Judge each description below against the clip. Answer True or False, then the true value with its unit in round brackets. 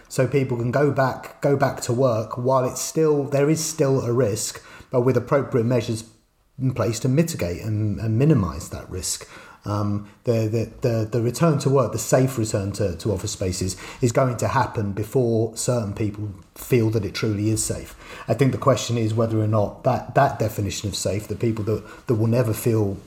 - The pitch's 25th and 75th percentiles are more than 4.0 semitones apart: False (3.5 semitones)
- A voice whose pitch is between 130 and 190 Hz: False (115 Hz)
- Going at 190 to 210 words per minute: True (205 wpm)